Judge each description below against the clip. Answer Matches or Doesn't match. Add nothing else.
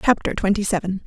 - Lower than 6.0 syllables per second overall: Doesn't match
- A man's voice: Doesn't match